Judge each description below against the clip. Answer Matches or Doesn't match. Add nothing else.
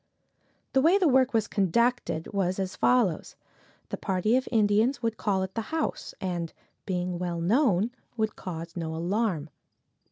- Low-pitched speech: Doesn't match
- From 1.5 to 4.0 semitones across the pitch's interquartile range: Doesn't match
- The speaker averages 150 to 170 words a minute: Matches